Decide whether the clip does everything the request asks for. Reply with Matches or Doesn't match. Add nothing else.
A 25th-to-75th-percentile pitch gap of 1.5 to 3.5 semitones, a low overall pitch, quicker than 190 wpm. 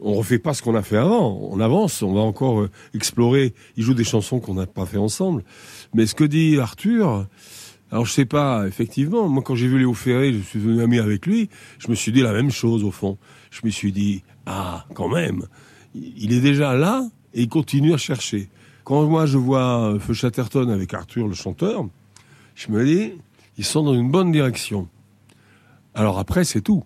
Doesn't match